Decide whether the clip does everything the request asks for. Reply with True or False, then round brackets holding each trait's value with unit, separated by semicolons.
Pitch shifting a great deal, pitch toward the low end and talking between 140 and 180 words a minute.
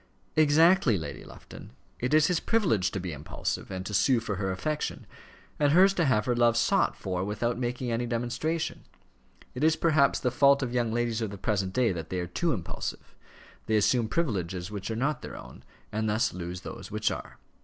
False (6.7 semitones; 120 Hz; 200 wpm)